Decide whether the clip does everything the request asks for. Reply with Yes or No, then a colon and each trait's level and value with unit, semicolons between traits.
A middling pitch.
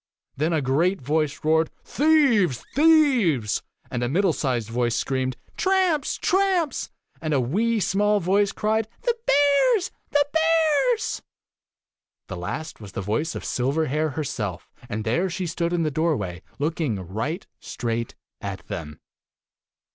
Yes: medium, 160 Hz